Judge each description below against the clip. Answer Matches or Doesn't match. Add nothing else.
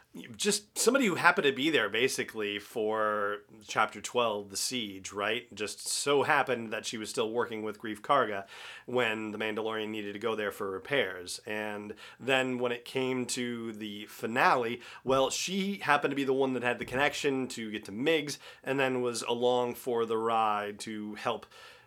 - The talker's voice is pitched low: Matches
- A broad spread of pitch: Doesn't match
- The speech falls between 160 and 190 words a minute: Matches